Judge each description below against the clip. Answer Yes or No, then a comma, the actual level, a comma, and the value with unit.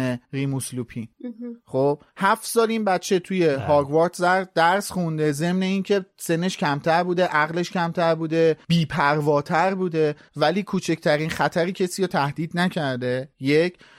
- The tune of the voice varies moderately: Yes, average, 3.9 semitones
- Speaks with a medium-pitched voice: Yes, medium, 165 Hz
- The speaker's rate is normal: Yes, average, 120 wpm